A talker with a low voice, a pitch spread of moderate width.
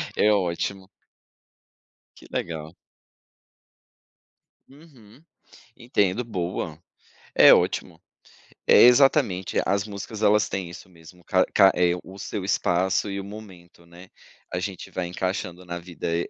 Yes: very low, 95 Hz; average, 3.0 semitones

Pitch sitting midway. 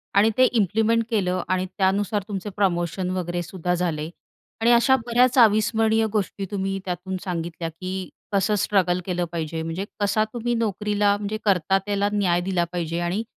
No: high, 195 Hz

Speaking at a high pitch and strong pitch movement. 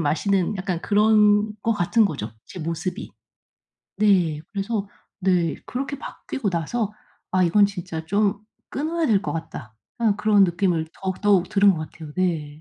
No: high, 195 Hz; average, 3.8 semitones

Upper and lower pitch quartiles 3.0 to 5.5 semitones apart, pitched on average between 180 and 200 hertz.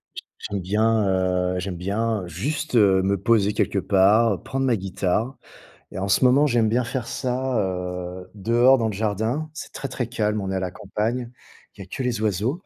No: average, 4.0 semitones; low, 105 Hz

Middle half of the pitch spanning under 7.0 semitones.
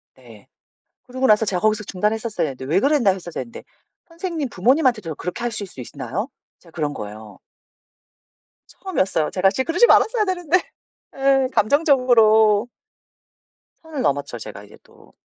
No: wide, 7.3 semitones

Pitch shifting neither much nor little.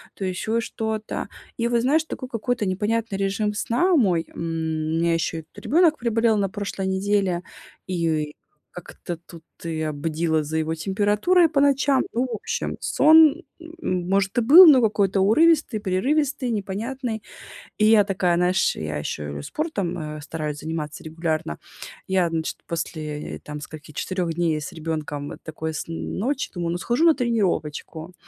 No: wide, 6.5 semitones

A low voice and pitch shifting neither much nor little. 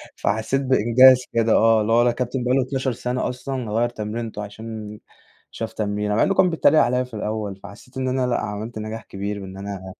Yes: low, 115 Hz; average, 3.2 semitones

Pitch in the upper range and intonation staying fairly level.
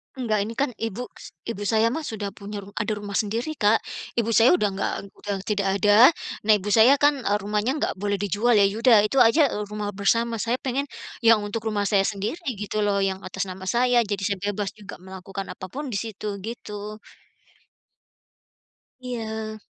Yes: high, 210 Hz; narrow, 2.3 semitones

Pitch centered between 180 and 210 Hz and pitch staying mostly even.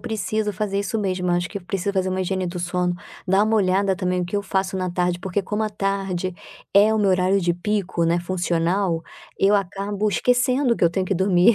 Yes: high, 190 Hz; narrow, 2.3 semitones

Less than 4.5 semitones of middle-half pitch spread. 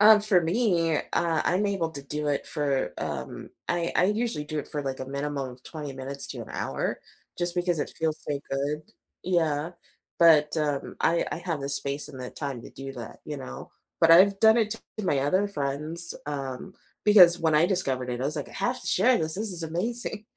No: average, 4.8 semitones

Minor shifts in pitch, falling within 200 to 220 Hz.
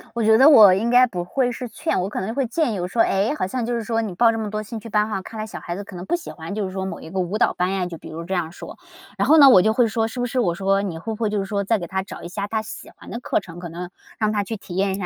No: average, 3.5 semitones; high, 205 Hz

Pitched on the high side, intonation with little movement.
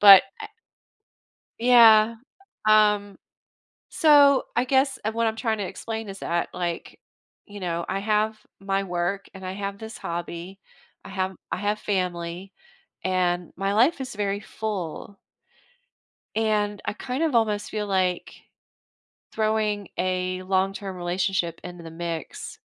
No: high, 200 Hz; average, 3.0 semitones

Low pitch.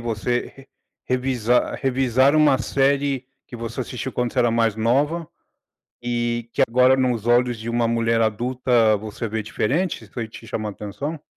Yes: low, 120 Hz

